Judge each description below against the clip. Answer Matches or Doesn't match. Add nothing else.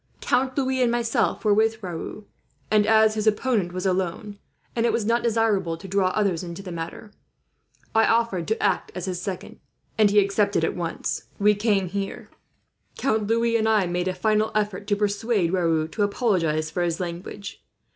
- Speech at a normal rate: Matches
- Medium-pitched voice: Doesn't match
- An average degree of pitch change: Matches